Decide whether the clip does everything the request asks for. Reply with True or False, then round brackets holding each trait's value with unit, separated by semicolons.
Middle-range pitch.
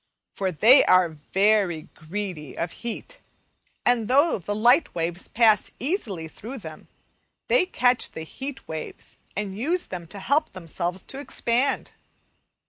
False (210 Hz)